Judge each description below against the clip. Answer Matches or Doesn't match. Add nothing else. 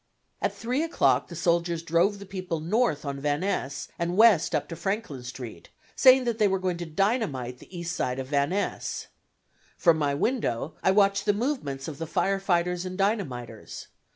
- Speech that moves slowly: Doesn't match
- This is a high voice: Doesn't match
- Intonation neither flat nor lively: Doesn't match